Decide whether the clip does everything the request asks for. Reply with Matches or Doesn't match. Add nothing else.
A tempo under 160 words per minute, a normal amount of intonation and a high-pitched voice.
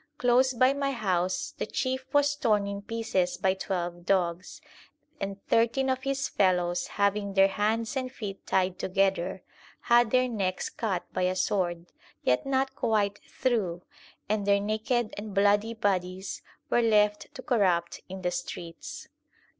Matches